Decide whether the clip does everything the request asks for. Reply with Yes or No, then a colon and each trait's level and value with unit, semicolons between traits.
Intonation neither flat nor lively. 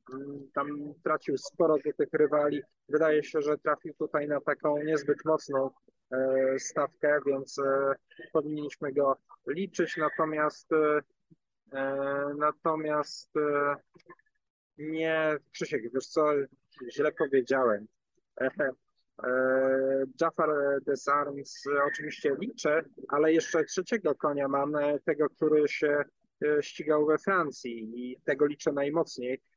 No: narrow, 1.9 semitones